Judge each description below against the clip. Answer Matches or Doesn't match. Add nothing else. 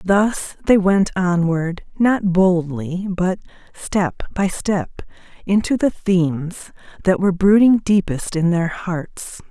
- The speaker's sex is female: Matches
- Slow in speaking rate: Matches